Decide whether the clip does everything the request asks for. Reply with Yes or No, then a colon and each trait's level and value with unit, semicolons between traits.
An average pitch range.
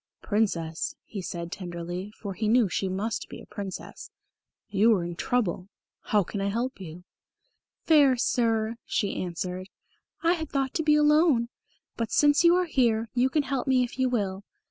No: wide, 5.7 semitones